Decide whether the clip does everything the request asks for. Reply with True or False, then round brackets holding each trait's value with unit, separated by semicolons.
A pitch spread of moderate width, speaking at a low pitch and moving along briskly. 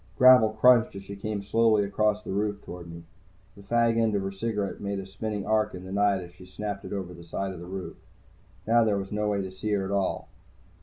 False (1.9 semitones; 100 Hz; 245 wpm)